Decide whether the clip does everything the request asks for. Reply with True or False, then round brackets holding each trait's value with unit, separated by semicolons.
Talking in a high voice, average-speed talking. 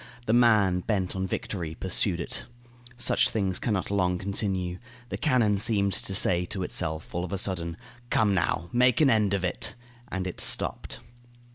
False (95 Hz; 175 wpm)